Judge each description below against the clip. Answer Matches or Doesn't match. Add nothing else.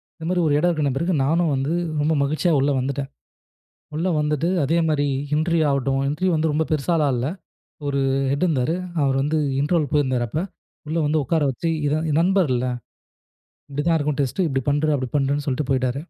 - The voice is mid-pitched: Matches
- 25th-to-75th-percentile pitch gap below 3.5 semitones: Matches